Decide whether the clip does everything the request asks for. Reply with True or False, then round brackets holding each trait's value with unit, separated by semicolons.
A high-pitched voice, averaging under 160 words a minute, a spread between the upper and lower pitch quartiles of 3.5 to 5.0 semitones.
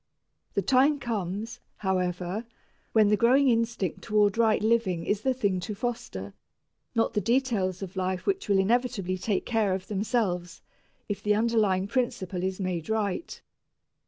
True (205 Hz; 150 wpm; 3.8 semitones)